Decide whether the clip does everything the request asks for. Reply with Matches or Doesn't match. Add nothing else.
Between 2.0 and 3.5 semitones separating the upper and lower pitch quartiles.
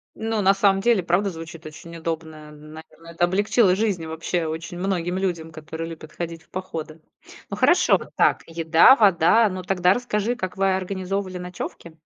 Matches